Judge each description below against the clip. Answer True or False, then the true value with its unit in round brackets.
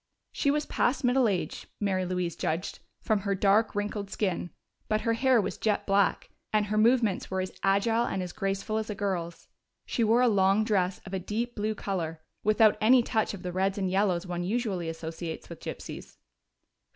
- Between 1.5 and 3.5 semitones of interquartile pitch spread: True (2.9 semitones)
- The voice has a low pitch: False (200 Hz)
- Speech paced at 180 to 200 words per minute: True (190 wpm)